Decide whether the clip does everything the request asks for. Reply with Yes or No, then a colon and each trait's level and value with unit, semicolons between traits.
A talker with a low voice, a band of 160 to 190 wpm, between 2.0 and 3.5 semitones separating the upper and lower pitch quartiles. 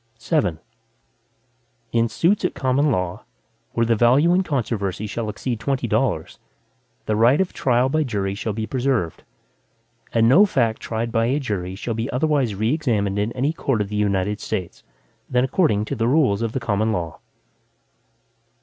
No: low, 115 Hz; average, 170 wpm; average, 4.3 semitones